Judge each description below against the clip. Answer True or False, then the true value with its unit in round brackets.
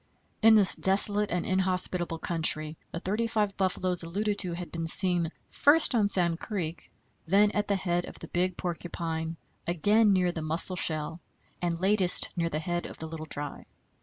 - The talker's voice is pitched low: False (180 Hz)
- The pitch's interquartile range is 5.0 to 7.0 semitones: False (3.1 semitones)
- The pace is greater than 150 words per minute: True (170 wpm)